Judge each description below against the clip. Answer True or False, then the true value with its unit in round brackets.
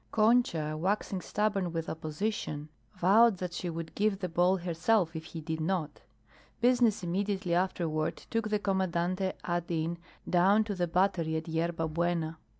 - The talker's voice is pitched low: False (175 Hz)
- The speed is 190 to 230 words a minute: False (150 wpm)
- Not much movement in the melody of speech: False (3.3 semitones)